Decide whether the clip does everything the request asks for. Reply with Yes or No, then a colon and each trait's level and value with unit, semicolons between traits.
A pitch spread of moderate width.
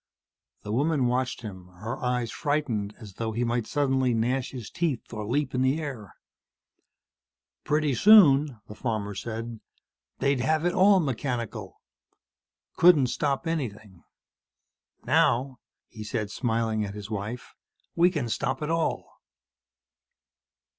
Yes: average, 4.9 semitones